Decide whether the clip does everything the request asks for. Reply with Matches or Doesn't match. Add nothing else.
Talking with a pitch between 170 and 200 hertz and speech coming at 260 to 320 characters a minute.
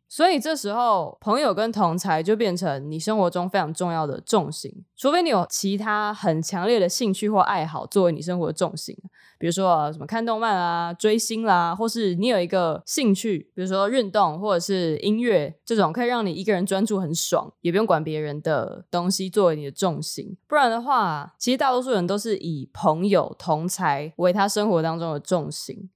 Matches